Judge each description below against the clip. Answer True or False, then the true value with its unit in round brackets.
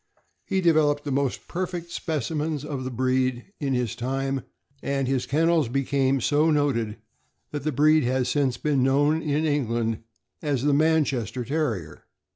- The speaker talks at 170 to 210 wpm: False (150 wpm)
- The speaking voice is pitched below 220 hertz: True (140 Hz)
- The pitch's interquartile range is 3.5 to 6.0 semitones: False (3.0 semitones)